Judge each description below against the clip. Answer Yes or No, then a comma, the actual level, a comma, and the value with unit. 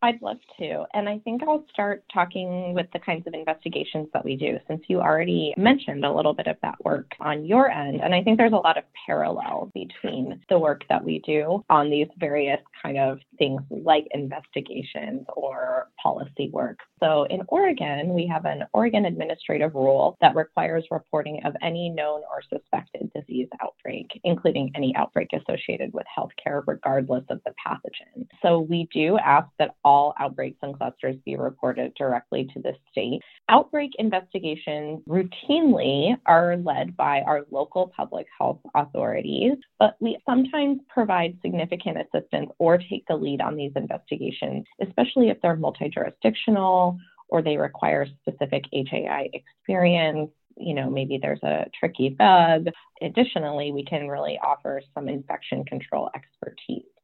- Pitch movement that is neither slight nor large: No, wide, 6.0 semitones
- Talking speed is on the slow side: No, average, 160 wpm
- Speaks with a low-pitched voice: No, medium, 170 Hz